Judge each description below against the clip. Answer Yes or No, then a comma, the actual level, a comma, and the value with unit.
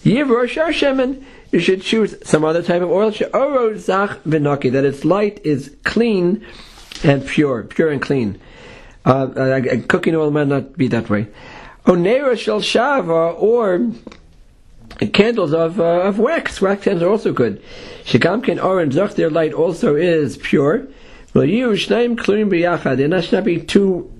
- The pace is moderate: No, slow, 120 wpm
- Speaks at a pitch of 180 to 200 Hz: Yes, medium, 185 Hz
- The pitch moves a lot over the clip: Yes, wide, 6.8 semitones